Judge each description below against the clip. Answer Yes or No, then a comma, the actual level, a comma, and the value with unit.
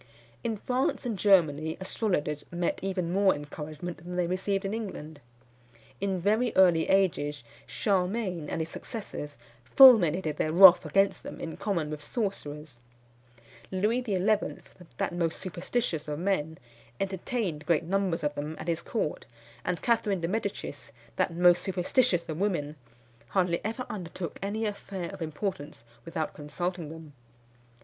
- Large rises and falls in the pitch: No, average, 3.9 semitones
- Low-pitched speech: No, medium, 180 Hz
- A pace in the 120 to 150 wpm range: Yes, average, 140 wpm